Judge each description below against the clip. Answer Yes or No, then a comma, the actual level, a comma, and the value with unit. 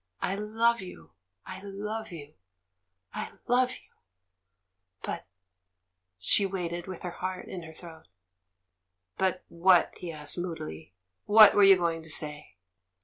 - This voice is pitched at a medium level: Yes, medium, 175 Hz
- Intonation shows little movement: No, average, 4.3 semitones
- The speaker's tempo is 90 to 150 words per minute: Yes, average, 145 wpm